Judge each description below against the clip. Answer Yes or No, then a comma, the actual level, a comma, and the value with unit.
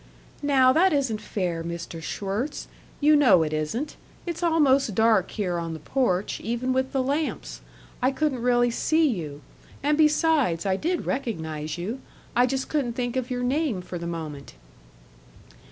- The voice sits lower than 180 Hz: No, high, 245 Hz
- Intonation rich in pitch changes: Yes, wide, 7.9 semitones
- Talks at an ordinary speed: Yes, average, 160 wpm